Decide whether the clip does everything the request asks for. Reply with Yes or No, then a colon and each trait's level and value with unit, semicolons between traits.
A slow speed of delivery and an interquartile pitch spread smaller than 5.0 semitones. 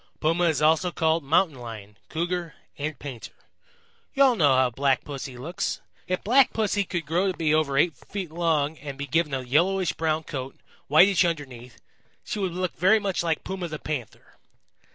No: average, 180 wpm; average, 4.3 semitones